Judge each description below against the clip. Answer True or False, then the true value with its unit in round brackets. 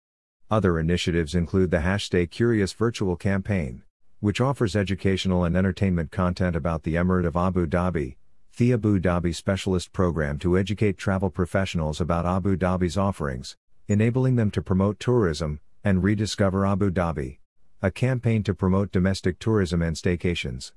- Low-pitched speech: True (95 Hz)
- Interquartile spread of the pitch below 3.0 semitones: True (2.6 semitones)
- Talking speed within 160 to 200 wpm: False (145 wpm)